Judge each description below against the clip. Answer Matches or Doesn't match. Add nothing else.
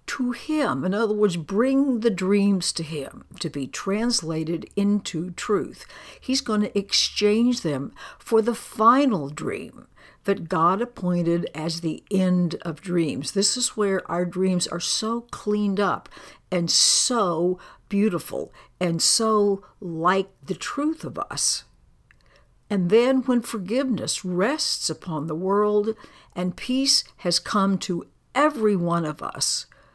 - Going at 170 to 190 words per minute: Doesn't match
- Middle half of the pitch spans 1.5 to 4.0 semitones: Doesn't match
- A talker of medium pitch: Doesn't match